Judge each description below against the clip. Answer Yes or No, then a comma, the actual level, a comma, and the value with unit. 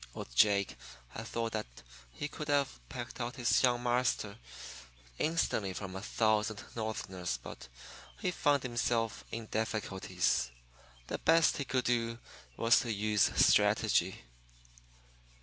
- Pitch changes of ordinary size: Yes, average, 3.0 semitones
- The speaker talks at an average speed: No, slow, 130 wpm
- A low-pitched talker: Yes, low, 115 Hz